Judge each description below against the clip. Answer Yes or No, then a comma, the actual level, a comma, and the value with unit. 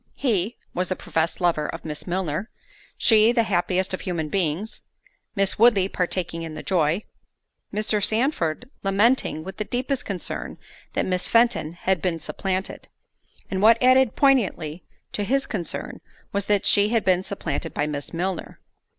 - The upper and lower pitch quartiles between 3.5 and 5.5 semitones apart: Yes, average, 4.2 semitones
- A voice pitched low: No, high, 190 Hz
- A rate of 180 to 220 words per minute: No, average, 145 wpm